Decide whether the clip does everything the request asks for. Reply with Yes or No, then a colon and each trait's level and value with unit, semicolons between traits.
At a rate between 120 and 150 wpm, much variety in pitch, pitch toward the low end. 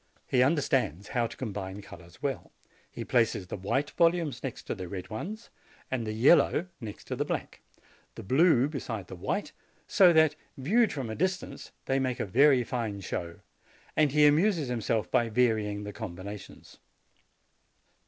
No: average, 165 wpm; wide, 6.2 semitones; low, 125 Hz